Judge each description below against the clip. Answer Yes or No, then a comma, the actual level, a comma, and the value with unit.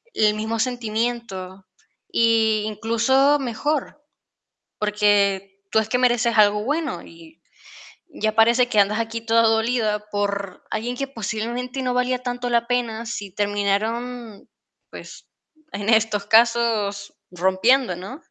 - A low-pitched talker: No, high, 225 Hz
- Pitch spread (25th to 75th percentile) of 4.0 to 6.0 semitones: No, average, 2.8 semitones